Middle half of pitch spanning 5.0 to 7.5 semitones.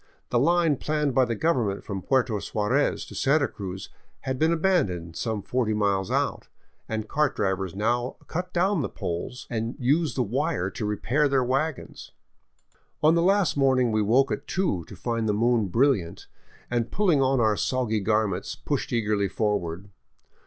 Yes: wide, 5.4 semitones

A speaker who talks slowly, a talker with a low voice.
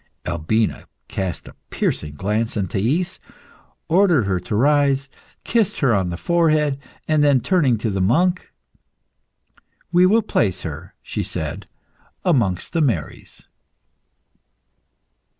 Yes: slow, 120 wpm; low, 125 Hz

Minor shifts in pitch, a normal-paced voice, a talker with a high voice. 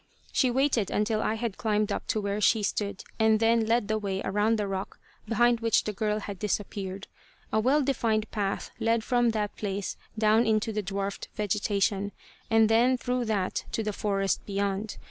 Yes: narrow, 2.0 semitones; average, 185 wpm; high, 215 Hz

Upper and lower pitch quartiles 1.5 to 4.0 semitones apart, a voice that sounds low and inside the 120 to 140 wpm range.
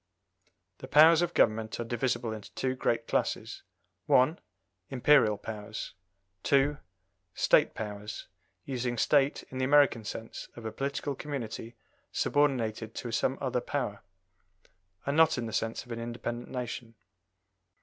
Yes: average, 3.5 semitones; low, 120 Hz; slow, 135 wpm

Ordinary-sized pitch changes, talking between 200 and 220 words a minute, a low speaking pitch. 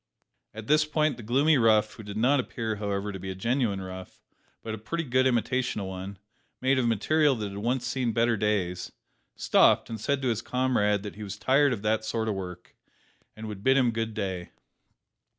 Yes: average, 4.0 semitones; fast, 205 wpm; low, 110 Hz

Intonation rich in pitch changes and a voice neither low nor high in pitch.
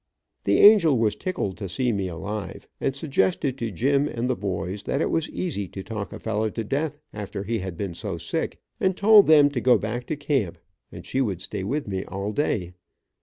No: wide, 6.4 semitones; low, 115 Hz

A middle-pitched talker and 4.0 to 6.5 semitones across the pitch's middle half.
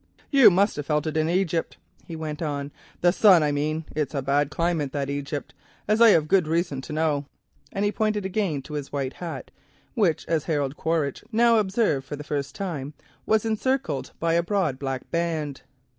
Yes: medium, 160 Hz; average, 4.7 semitones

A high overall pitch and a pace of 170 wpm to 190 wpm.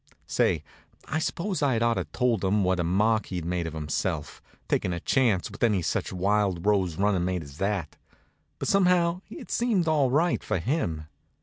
No: low, 105 Hz; average, 185 wpm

